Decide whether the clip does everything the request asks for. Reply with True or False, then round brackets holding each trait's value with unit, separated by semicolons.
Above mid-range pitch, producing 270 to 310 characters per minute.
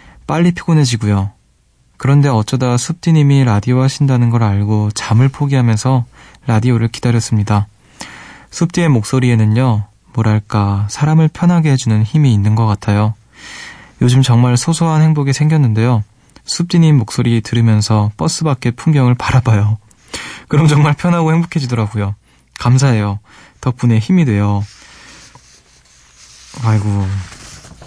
False (120 Hz; 300 characters per minute)